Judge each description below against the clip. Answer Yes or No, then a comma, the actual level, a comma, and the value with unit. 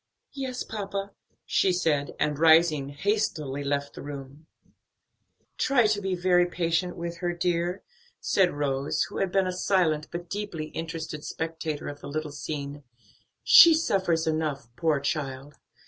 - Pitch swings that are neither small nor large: Yes, average, 4.0 semitones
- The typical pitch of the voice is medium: Yes, medium, 165 Hz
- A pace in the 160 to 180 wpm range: No, average, 145 wpm